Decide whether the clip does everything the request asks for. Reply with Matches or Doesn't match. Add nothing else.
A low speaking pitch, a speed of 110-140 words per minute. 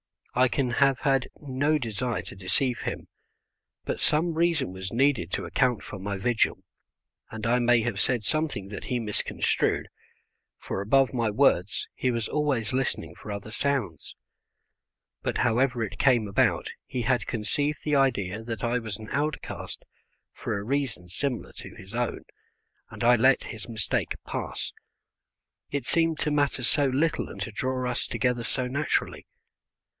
Doesn't match